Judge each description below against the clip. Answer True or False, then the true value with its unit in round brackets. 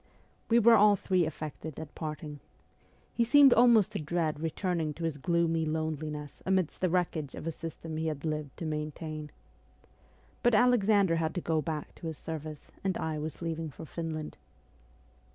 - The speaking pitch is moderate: True (160 Hz)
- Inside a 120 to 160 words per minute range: False (170 wpm)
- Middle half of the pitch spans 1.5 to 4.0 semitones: True (2.9 semitones)